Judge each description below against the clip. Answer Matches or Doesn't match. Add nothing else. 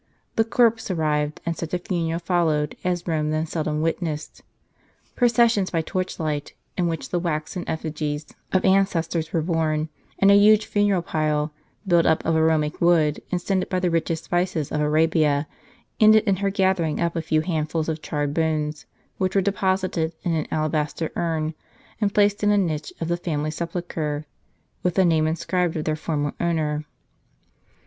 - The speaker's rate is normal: Matches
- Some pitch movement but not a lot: Matches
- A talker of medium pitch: Matches